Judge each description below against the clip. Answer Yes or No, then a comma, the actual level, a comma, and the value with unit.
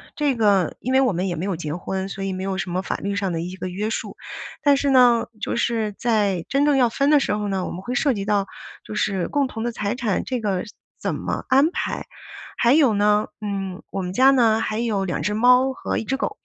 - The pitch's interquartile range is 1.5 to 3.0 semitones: No, average, 4.6 semitones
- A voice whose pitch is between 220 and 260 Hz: No, high, 210 Hz